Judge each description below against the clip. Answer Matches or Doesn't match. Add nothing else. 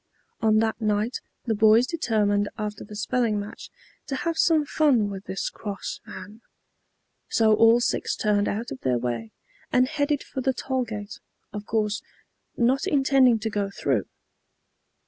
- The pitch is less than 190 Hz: Doesn't match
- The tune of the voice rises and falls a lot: Doesn't match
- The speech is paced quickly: Doesn't match